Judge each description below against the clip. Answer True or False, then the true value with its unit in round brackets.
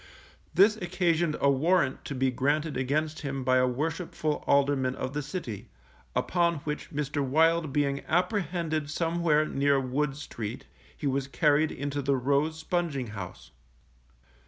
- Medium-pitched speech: True (145 Hz)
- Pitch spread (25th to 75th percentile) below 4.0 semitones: True (3.2 semitones)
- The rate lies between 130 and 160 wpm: True (140 wpm)